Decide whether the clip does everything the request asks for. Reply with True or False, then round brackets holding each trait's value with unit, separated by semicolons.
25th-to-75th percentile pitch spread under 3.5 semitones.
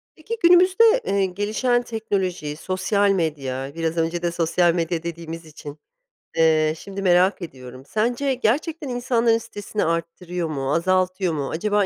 False (4.8 semitones)